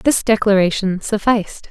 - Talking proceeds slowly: Yes, slow, 105 wpm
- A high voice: Yes, high, 205 Hz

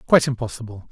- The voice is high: No, low, 120 Hz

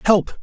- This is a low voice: No, high, 195 Hz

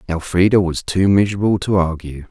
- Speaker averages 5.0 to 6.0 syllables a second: Yes, 5.6 syllables/s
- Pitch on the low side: Yes, very low, 90 Hz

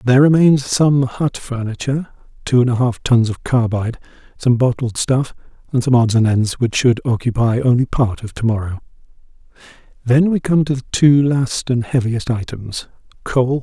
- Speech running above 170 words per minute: Yes, average, 180 wpm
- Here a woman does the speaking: No, male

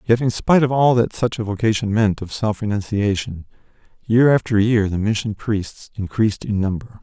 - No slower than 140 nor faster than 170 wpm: No, average, 190 wpm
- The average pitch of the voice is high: No, low, 110 Hz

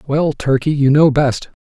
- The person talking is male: Yes, male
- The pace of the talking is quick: No, average, 185 wpm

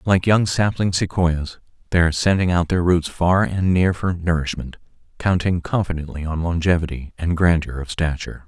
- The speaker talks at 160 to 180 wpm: Yes, average, 165 wpm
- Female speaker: No, male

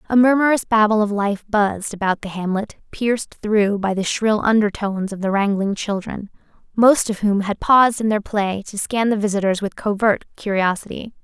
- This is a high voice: Yes, high, 210 Hz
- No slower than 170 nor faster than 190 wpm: Yes, average, 180 wpm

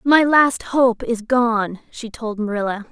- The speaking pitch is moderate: No, high, 235 Hz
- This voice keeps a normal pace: Yes, average, 165 wpm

